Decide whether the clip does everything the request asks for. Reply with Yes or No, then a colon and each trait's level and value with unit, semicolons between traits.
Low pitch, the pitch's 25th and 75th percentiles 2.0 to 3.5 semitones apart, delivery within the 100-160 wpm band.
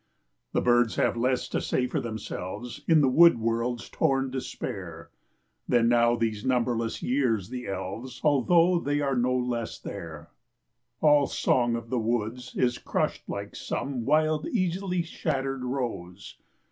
Yes: low, 125 Hz; average, 3.0 semitones; average, 145 wpm